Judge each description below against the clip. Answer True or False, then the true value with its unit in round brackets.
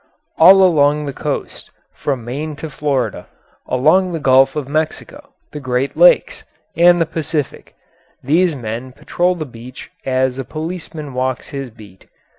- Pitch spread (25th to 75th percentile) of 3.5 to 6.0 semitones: True (4.1 semitones)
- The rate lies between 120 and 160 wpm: True (145 wpm)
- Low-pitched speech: False (145 Hz)